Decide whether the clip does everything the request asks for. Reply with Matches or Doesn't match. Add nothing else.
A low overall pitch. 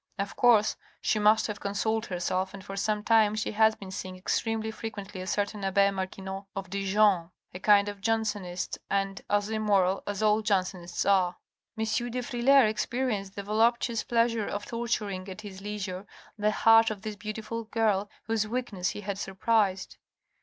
Doesn't match